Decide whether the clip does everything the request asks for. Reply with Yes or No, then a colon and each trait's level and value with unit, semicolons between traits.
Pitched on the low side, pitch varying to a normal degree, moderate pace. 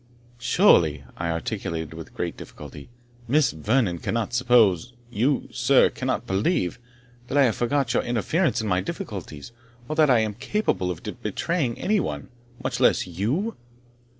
No: low, 115 Hz; wide, 7.5 semitones; average, 150 wpm